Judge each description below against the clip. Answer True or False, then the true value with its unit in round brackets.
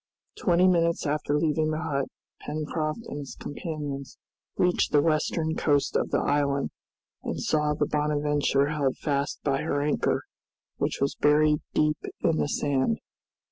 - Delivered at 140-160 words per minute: True (145 wpm)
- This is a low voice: False (150 Hz)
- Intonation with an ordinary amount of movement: False (1.5 semitones)